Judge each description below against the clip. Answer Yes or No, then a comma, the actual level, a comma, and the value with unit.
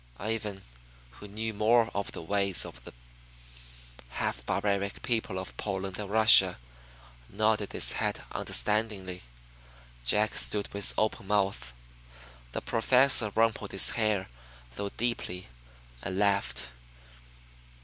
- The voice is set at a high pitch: No, low, 100 Hz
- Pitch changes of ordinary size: No, narrow, 2.2 semitones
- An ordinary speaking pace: No, slow, 115 wpm